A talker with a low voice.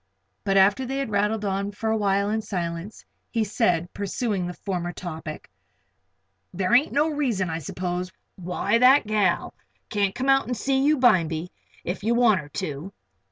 No: high, 200 Hz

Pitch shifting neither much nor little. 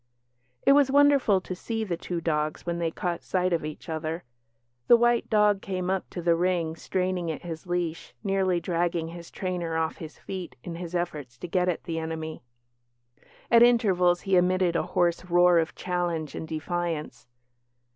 No: narrow, 2.1 semitones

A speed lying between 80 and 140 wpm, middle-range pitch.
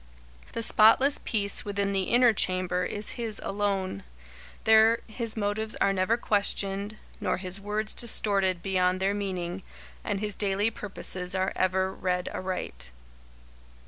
No: slow, 135 wpm; high, 200 Hz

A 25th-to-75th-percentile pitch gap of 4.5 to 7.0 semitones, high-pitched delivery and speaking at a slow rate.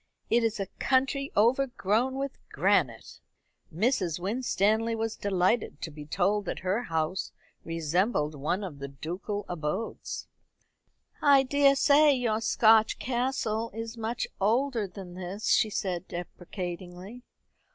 Yes: average, 5.3 semitones; high, 210 Hz; slow, 120 wpm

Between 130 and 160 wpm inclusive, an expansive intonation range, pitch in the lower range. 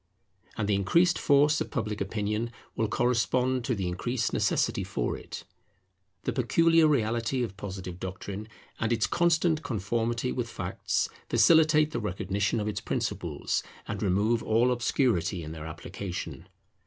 No: average, 140 wpm; average, 4.5 semitones; low, 115 Hz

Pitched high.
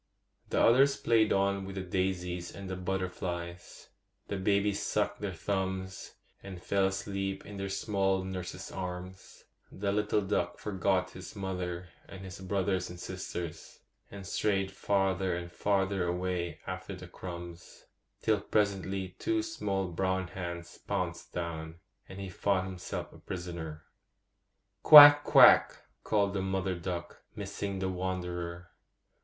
No: very low, 95 Hz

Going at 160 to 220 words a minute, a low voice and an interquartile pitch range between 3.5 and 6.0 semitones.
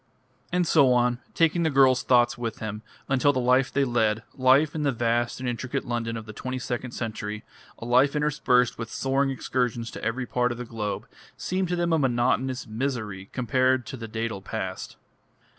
No: average, 190 wpm; low, 125 Hz; average, 2.7 semitones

